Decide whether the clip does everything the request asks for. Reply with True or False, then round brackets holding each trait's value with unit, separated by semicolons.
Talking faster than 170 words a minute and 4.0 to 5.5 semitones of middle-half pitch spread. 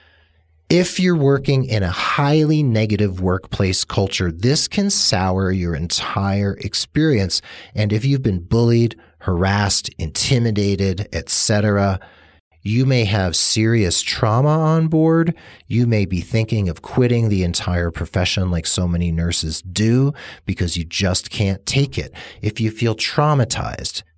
False (135 wpm; 5.2 semitones)